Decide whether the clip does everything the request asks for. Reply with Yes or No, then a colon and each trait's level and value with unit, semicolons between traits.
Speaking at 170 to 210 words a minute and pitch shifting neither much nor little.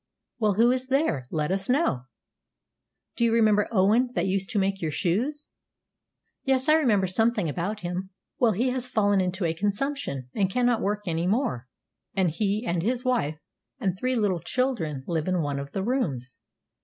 No: average, 180 wpm; wide, 5.9 semitones